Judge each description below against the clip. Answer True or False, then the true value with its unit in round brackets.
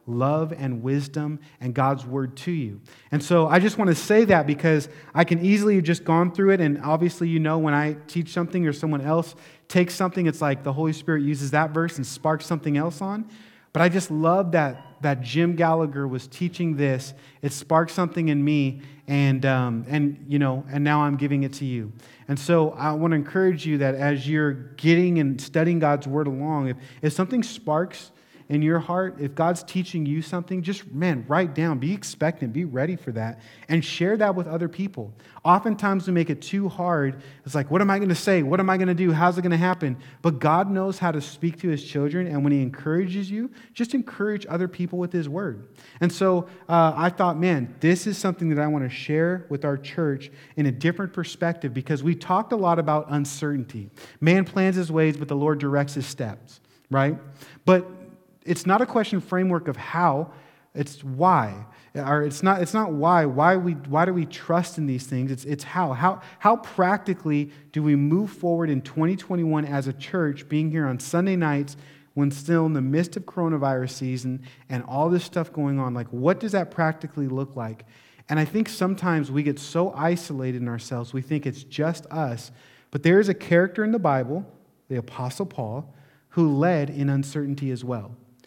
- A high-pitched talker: False (155 Hz)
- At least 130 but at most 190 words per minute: False (205 wpm)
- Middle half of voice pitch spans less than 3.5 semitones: False (4.0 semitones)